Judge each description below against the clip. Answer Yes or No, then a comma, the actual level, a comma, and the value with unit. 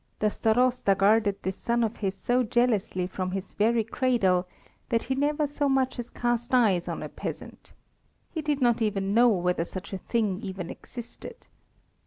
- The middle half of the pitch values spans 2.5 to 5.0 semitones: Yes, average, 4.2 semitones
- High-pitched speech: Yes, high, 225 Hz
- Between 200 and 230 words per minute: No, average, 175 wpm